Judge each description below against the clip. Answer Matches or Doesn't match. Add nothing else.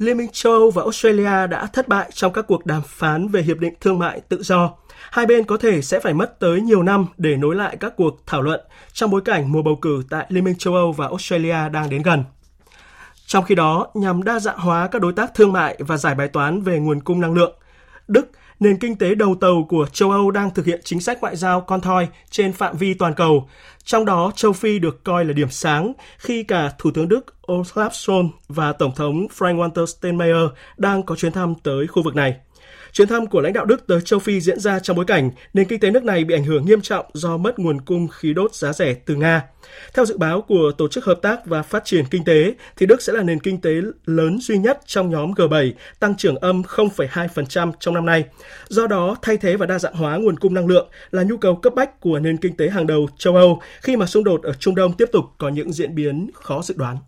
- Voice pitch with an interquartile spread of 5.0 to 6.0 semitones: Doesn't match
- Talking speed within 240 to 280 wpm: Matches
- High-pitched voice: Doesn't match